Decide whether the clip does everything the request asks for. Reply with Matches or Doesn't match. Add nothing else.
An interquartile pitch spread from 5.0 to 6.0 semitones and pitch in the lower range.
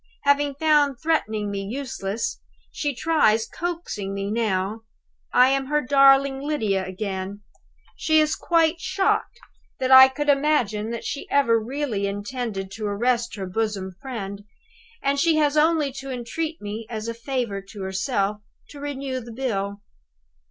Doesn't match